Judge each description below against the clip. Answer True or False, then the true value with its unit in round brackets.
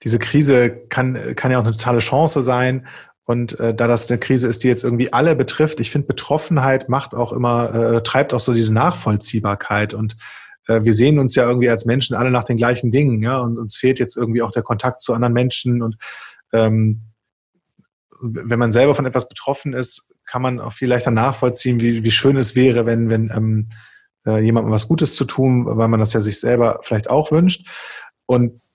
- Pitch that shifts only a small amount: True (2.2 semitones)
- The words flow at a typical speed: False (205 wpm)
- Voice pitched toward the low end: True (120 Hz)